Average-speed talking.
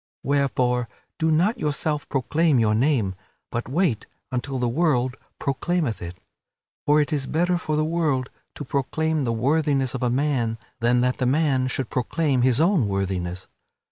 Yes: average, 160 wpm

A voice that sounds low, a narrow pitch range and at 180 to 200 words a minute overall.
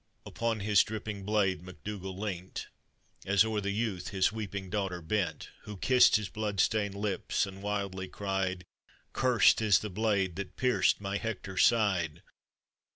No: low, 100 Hz; narrow, 2.2 semitones; average, 155 wpm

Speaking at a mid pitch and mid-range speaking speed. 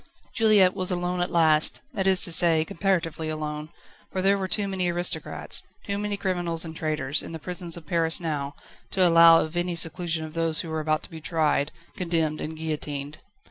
Yes: medium, 165 Hz; average, 195 wpm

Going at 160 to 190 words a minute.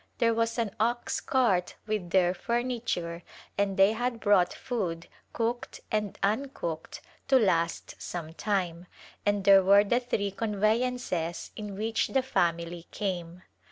No: average, 145 wpm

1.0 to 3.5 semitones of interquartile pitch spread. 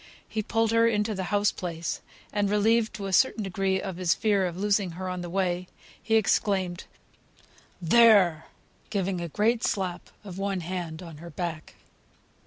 Yes: average, 3.0 semitones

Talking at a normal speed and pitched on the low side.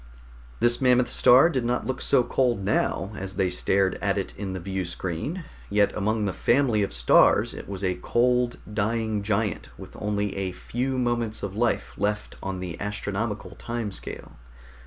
Yes: average, 170 wpm; low, 105 Hz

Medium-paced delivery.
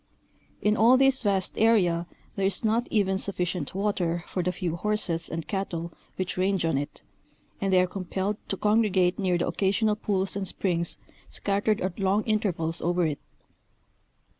Yes: average, 165 wpm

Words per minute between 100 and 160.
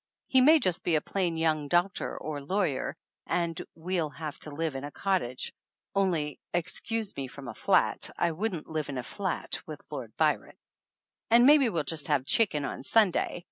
No: average, 180 wpm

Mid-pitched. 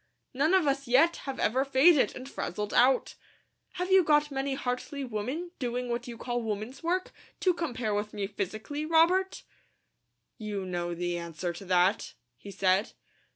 No: very high, 250 Hz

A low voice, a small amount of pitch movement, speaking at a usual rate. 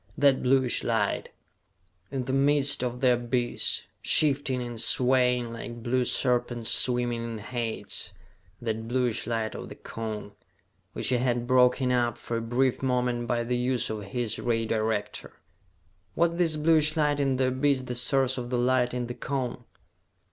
Yes: low, 125 Hz; narrow, 1.7 semitones; average, 160 wpm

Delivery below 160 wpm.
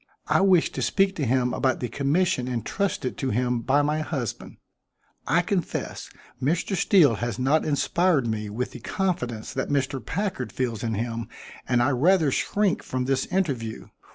No: average, 165 wpm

